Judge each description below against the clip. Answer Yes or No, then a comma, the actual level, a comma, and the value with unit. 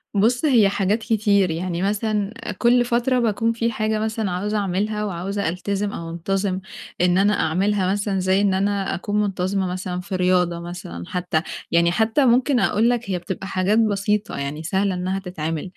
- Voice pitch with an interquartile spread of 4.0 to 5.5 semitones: No, average, 3.0 semitones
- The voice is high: Yes, high, 195 Hz